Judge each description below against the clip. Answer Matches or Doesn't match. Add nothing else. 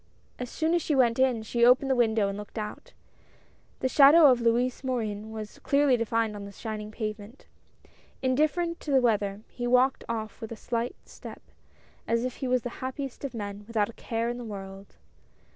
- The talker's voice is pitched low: Doesn't match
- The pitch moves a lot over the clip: Doesn't match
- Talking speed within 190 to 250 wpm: Matches